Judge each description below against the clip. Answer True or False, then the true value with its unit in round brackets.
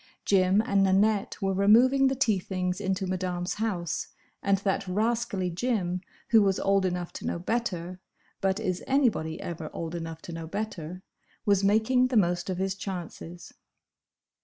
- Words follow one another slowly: False (150 wpm)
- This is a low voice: False (190 Hz)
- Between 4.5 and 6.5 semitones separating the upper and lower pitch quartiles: False (3.1 semitones)